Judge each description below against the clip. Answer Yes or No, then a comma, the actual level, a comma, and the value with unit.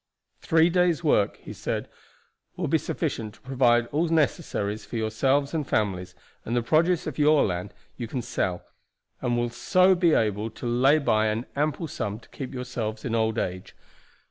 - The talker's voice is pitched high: No, low, 120 Hz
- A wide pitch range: Yes, wide, 5.9 semitones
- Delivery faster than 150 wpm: Yes, average, 175 wpm